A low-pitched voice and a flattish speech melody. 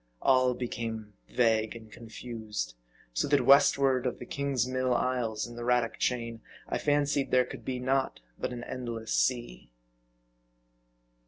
Yes: low, 125 Hz; narrow, 2.0 semitones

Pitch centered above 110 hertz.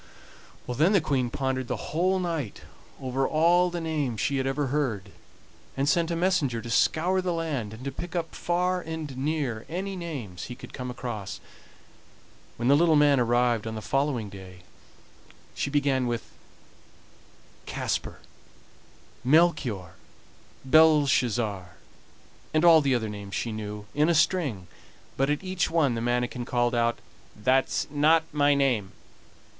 Yes: low, 135 Hz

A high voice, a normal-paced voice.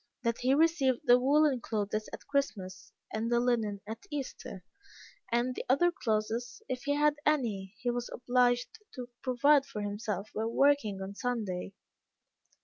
Yes: high, 245 Hz; average, 155 wpm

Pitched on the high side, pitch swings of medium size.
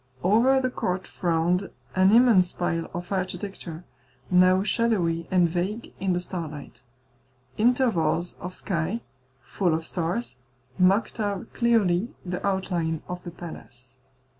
No: medium, 180 Hz; average, 3.1 semitones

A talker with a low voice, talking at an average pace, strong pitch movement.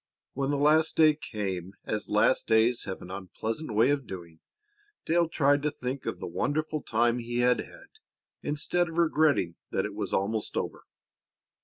Yes: low, 125 Hz; average, 170 wpm; wide, 6.2 semitones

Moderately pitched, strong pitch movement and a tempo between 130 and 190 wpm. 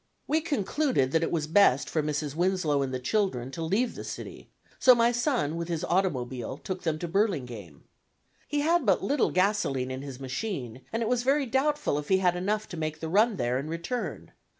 No: medium, 175 Hz; wide, 8.0 semitones; fast, 205 wpm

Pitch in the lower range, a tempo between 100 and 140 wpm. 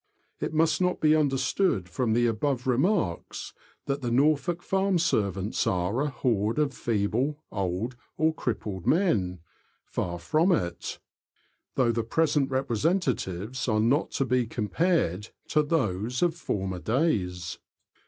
Yes: low, 125 Hz; slow, 135 wpm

